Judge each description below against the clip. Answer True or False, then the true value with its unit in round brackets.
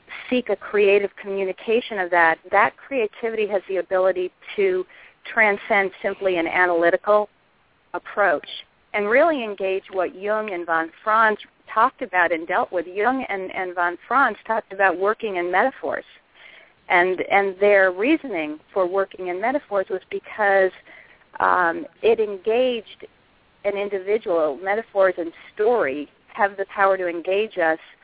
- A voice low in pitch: False (200 Hz)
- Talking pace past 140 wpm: False (135 wpm)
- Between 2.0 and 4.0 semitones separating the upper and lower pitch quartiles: True (3.3 semitones)